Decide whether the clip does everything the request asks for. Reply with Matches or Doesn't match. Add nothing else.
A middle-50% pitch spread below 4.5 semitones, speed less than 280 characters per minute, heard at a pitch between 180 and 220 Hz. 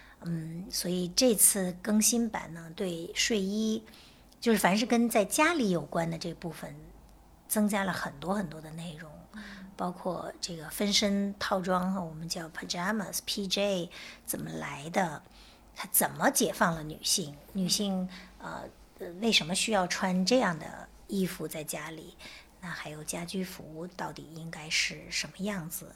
Matches